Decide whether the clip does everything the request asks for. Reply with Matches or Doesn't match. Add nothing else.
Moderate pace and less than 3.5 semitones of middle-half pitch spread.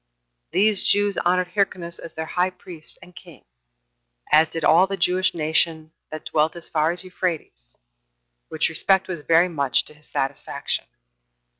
Matches